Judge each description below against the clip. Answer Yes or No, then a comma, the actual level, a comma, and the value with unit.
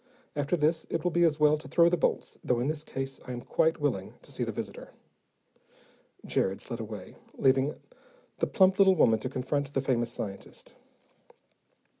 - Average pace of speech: Yes, average, 180 wpm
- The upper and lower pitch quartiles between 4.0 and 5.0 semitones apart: Yes, average, 4.7 semitones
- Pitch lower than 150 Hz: Yes, medium, 140 Hz